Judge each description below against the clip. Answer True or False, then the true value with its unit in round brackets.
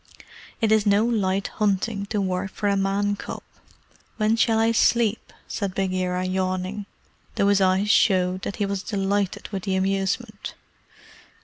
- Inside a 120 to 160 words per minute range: True (150 wpm)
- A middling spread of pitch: False (1.9 semitones)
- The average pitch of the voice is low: False (200 Hz)